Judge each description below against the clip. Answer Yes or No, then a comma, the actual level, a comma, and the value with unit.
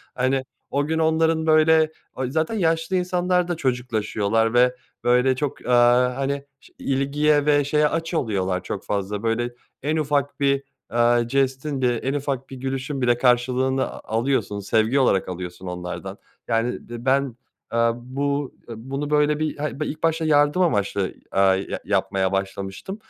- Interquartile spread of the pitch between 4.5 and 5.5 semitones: No, average, 4.0 semitones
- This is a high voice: No, low, 135 Hz